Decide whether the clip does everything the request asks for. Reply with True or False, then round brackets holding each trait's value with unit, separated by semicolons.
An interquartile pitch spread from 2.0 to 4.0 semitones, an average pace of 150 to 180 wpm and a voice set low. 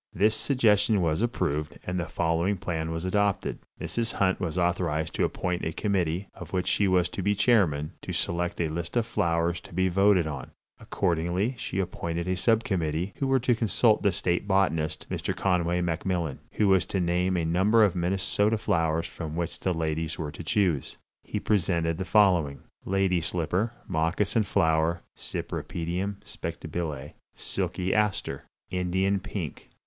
True (3.2 semitones; 160 wpm; 90 Hz)